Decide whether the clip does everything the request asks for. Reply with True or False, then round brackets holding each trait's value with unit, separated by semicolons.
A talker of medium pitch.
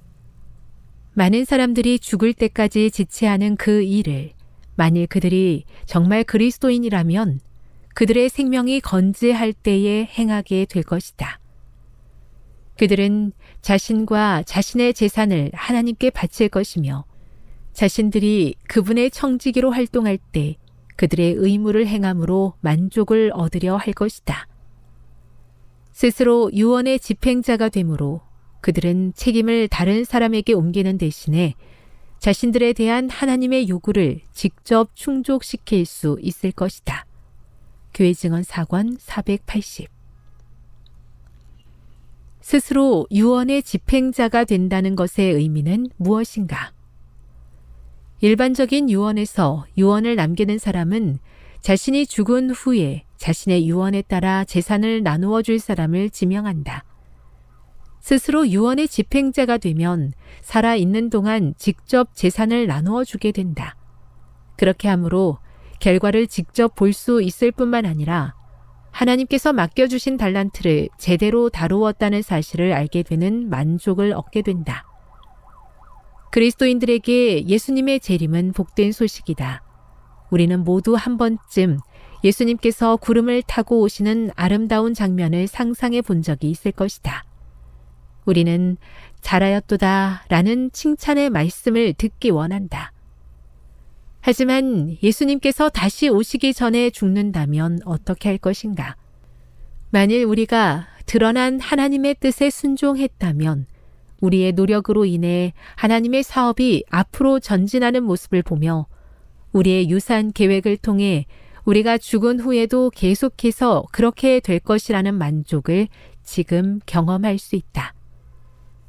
False (200 Hz)